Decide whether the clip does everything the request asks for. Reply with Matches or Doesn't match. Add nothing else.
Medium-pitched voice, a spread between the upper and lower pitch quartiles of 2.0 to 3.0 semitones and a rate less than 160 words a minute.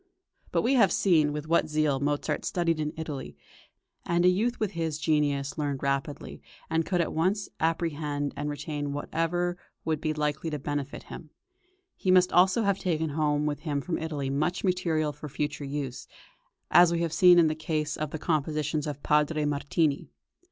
Doesn't match